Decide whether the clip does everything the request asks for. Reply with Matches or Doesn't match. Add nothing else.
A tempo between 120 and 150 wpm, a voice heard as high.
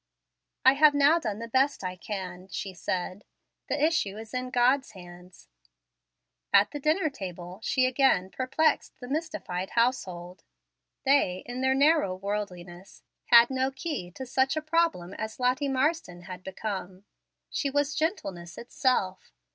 Matches